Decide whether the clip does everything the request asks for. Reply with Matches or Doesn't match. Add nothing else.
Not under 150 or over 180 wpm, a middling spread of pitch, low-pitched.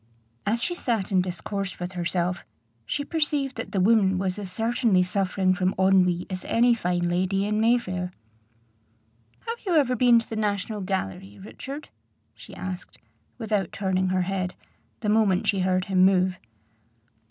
Doesn't match